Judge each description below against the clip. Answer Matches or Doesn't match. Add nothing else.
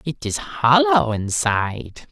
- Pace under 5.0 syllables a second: Matches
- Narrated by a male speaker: Matches